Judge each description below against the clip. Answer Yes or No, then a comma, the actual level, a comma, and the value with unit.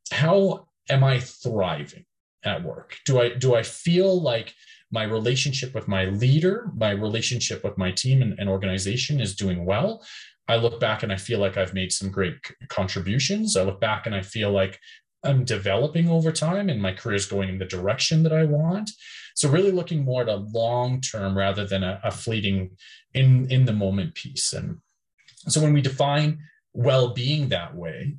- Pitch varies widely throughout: Yes, wide, 6.8 semitones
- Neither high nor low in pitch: No, low, 120 Hz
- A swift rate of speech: No, average, 185 wpm